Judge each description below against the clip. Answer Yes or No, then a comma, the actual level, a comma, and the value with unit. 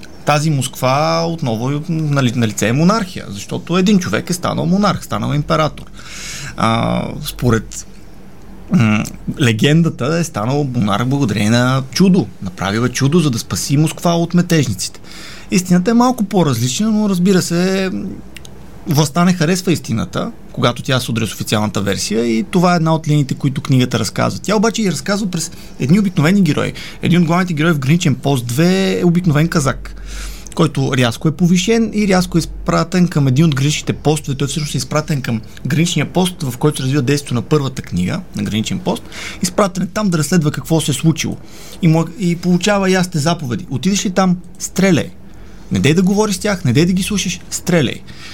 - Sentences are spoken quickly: Yes, fast, 170 wpm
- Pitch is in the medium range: Yes, medium, 155 Hz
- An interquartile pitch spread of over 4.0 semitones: Yes, average, 5.3 semitones